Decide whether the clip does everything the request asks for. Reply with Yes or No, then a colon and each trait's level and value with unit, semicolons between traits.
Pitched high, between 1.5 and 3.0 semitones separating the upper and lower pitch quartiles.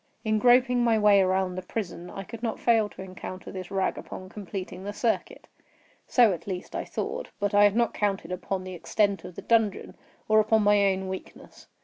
Yes: high, 200 Hz; average, 2.7 semitones